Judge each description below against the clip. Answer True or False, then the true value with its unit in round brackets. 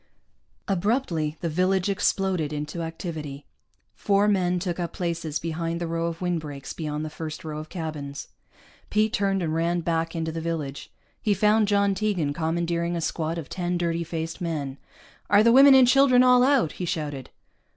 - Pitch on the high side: False (170 Hz)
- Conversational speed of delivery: True (170 wpm)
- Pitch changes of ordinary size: True (3.5 semitones)